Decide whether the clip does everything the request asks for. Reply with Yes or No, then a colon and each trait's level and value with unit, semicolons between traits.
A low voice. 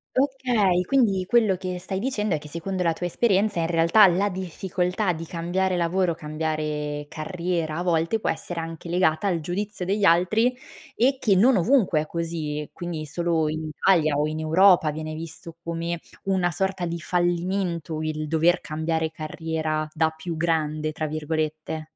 No: medium, 170 Hz